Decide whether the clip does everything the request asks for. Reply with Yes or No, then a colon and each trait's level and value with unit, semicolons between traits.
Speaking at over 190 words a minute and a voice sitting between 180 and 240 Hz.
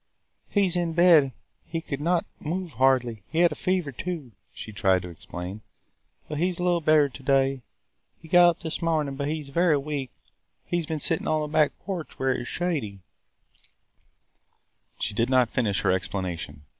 No: average, 200 wpm; medium, 150 Hz